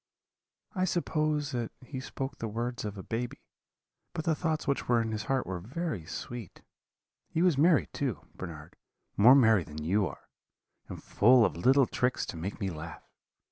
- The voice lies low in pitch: Yes, low, 120 Hz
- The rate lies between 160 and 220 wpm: Yes, average, 180 wpm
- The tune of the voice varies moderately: No, wide, 6.1 semitones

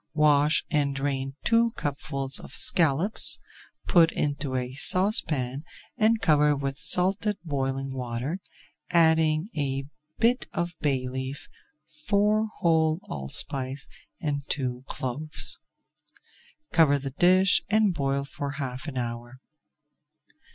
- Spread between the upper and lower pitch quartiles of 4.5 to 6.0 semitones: No, average, 4.0 semitones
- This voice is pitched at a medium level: Yes, medium, 145 Hz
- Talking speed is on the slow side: Yes, slow, 110 wpm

